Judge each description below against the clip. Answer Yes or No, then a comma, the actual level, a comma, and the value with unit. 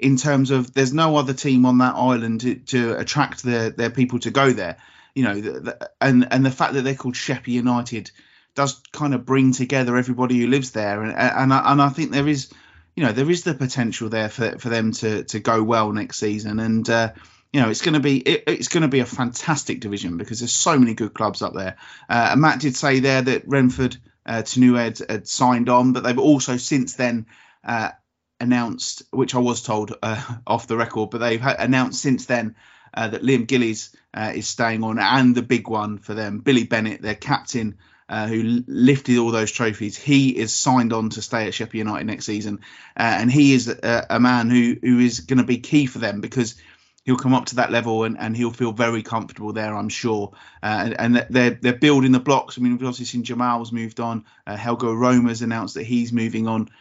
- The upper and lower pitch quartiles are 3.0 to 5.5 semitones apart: No, narrow, 2.6 semitones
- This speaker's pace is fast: Yes, fast, 225 wpm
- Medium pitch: No, low, 120 Hz